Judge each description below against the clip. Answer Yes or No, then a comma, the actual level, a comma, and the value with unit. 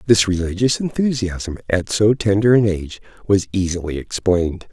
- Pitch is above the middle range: No, low, 100 Hz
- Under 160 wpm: Yes, average, 140 wpm